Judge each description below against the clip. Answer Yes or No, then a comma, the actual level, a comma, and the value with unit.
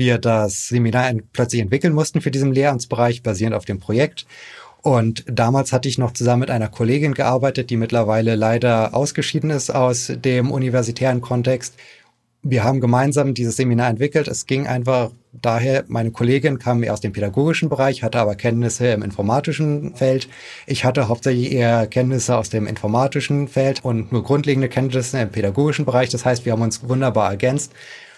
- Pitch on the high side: No, low, 125 Hz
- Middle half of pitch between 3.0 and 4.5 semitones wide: No, narrow, 2.5 semitones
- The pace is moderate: Yes, average, 170 wpm